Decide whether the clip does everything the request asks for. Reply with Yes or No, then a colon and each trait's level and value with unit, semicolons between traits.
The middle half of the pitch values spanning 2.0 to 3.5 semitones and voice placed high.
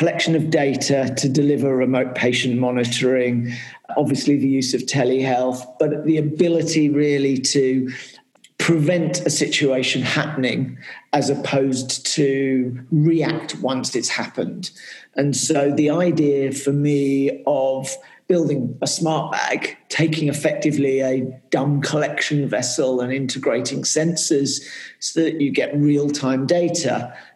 No: average, 2.8 semitones; medium, 140 Hz